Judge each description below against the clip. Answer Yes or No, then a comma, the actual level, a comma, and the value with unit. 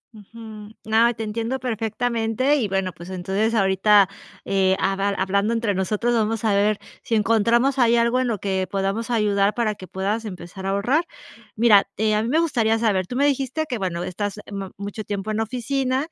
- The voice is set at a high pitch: Yes, high, 215 Hz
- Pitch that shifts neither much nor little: Yes, average, 3.0 semitones